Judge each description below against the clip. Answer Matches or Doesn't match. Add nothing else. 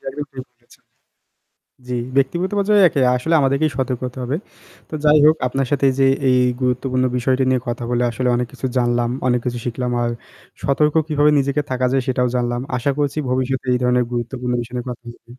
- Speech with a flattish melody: Matches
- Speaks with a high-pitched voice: Doesn't match